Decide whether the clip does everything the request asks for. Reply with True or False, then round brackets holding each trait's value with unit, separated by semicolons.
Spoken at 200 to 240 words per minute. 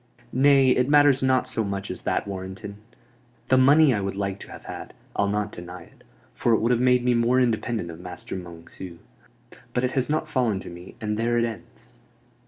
True (205 wpm)